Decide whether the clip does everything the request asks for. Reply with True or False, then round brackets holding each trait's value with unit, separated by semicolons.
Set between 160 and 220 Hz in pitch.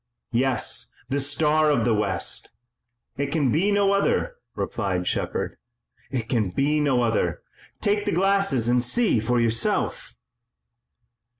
False (135 Hz)